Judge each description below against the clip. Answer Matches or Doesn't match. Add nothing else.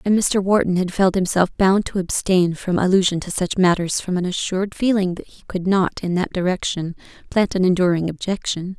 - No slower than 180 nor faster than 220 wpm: Matches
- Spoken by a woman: Matches